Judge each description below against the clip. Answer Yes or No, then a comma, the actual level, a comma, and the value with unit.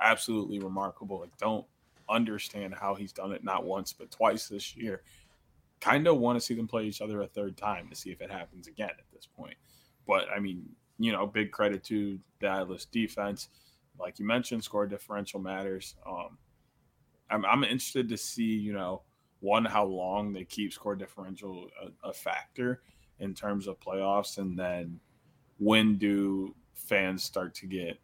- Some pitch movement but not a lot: No, narrow, 1.9 semitones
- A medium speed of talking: Yes, average, 175 wpm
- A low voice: Yes, low, 100 Hz